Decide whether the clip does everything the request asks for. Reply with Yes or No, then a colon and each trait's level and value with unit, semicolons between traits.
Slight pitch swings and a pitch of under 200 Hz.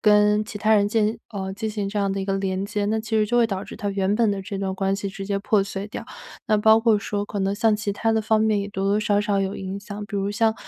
No: narrow, 1.6 semitones; high, 205 Hz